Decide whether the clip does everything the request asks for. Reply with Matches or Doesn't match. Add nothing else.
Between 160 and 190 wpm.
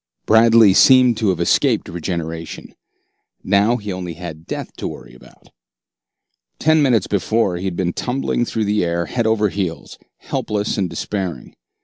Doesn't match